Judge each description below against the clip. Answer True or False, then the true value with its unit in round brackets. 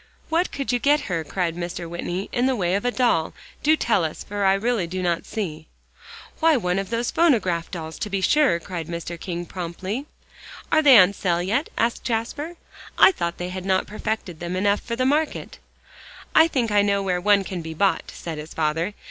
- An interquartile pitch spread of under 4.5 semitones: False (5.6 semitones)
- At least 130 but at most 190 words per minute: False (205 wpm)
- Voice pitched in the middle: False (195 Hz)